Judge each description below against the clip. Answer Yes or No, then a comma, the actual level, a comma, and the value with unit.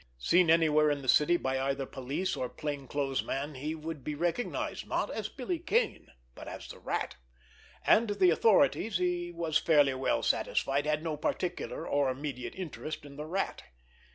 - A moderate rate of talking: Yes, average, 170 wpm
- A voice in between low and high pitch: Yes, medium, 150 Hz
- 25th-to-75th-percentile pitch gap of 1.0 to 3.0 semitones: No, average, 4.2 semitones